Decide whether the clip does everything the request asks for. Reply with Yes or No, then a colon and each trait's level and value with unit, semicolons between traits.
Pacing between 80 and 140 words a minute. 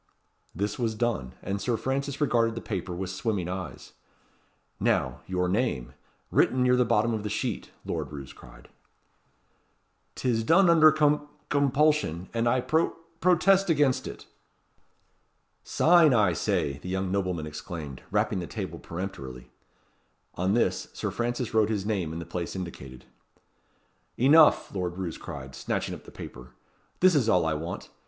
No: average, 150 wpm